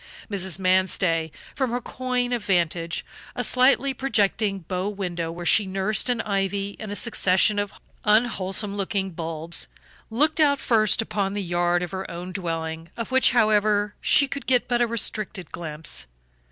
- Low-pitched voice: No, high, 200 Hz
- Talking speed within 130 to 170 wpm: Yes, average, 160 wpm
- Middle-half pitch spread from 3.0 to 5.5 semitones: Yes, average, 4.2 semitones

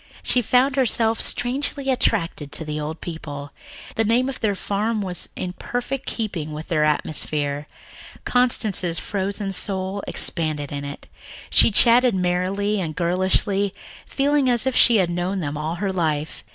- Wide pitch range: Yes, wide, 6.2 semitones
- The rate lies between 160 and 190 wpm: No, average, 150 wpm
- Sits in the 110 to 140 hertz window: No, high, 190 Hz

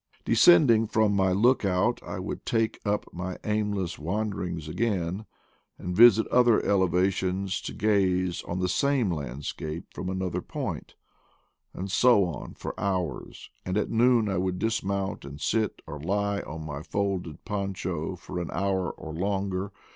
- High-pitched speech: No, very low, 95 Hz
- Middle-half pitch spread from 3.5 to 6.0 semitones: No, average, 2.9 semitones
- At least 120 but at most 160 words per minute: Yes, average, 150 wpm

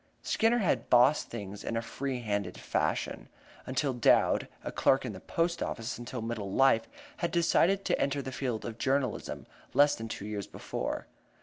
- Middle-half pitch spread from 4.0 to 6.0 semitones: Yes, average, 4.3 semitones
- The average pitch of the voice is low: Yes, low, 125 Hz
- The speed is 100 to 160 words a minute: No, average, 175 wpm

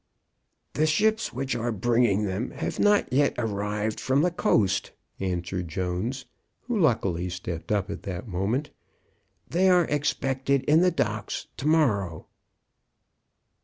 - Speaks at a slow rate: Yes, slow, 130 wpm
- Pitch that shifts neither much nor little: No, wide, 7.4 semitones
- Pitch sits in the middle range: No, low, 120 Hz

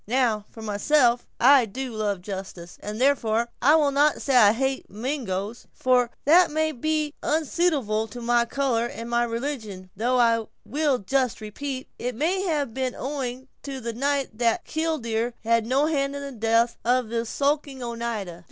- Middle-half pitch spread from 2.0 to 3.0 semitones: No, average, 3.8 semitones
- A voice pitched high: Yes, high, 245 Hz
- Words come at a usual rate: Yes, average, 170 wpm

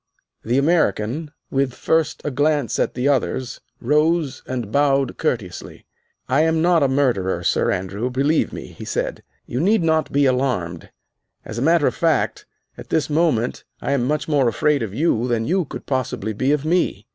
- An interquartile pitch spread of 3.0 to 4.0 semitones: No, average, 4.5 semitones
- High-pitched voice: No, low, 135 Hz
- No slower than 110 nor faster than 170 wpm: No, average, 180 wpm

